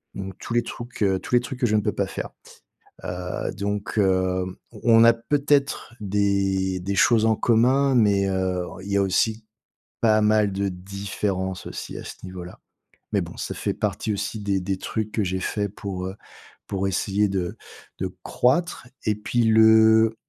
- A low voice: Yes, low, 100 Hz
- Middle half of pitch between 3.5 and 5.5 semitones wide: No, average, 2.9 semitones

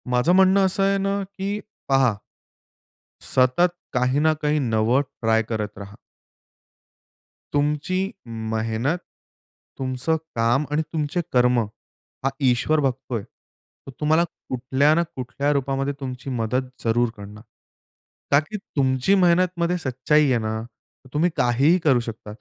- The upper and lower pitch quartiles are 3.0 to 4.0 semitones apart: No, average, 4.5 semitones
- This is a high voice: No, low, 135 Hz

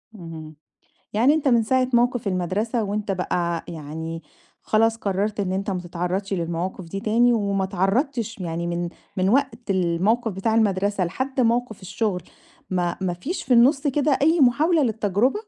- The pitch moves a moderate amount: Yes, average, 4.9 semitones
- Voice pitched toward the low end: No, high, 205 Hz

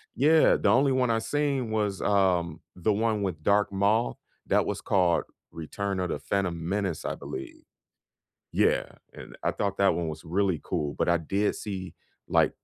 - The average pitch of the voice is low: Yes, low, 100 Hz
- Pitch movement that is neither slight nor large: Yes, average, 3.8 semitones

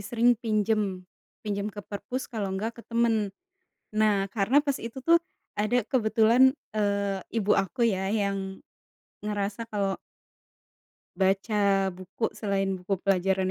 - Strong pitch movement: No, average, 2.7 semitones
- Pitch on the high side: Yes, high, 205 Hz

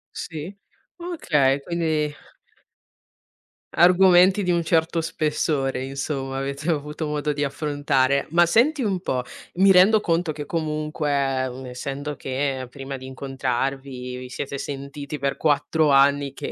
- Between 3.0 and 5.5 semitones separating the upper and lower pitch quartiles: Yes, average, 3.3 semitones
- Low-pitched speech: No, medium, 145 Hz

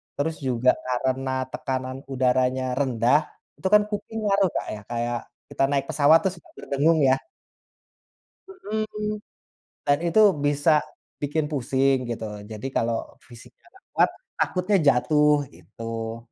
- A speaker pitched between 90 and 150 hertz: Yes, low, 135 Hz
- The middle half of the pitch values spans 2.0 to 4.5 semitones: No, average, 4.9 semitones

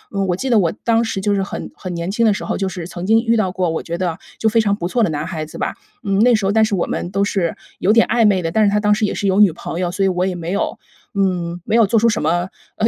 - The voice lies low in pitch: No, high, 195 Hz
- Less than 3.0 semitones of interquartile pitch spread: No, average, 3.4 semitones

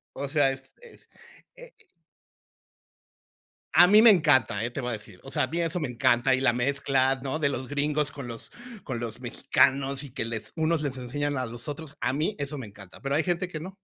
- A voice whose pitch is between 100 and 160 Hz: Yes, medium, 140 Hz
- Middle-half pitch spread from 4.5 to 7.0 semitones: No, average, 3.7 semitones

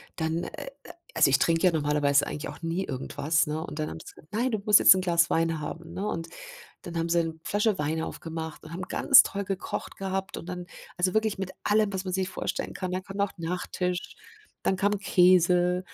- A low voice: No, medium, 175 Hz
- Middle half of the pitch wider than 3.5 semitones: No, average, 2.8 semitones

